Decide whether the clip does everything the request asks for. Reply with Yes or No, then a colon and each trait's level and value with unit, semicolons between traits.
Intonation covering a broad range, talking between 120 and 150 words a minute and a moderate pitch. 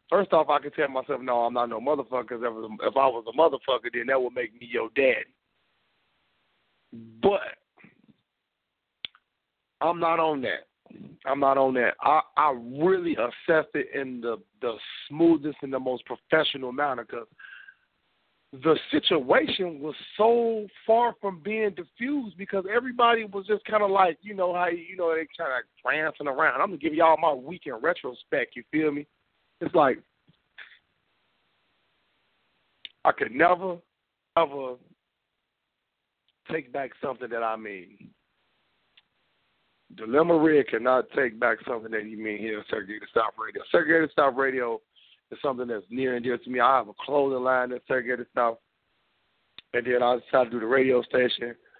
No: wide, 6.2 semitones; average, 160 wpm; medium, 145 Hz